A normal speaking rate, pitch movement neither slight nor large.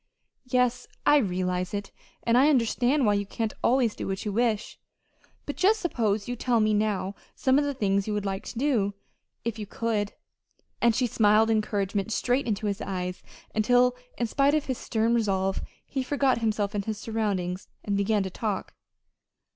Yes: average, 180 wpm; average, 3.5 semitones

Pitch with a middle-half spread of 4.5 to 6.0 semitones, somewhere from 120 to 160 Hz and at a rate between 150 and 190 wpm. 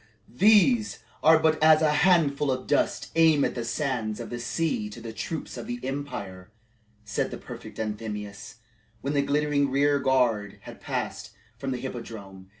Yes: wide, 5.5 semitones; low, 135 Hz; average, 160 wpm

